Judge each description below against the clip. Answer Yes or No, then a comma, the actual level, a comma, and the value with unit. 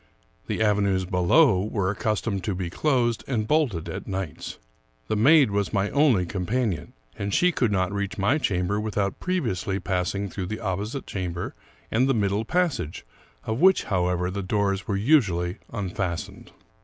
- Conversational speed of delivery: Yes, average, 160 wpm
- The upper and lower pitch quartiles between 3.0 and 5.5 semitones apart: Yes, average, 3.8 semitones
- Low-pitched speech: Yes, low, 100 Hz